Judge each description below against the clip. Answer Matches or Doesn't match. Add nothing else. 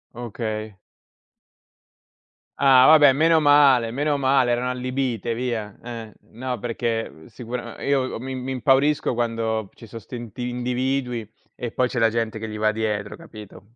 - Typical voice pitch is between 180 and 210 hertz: Doesn't match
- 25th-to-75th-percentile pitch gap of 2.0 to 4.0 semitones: Matches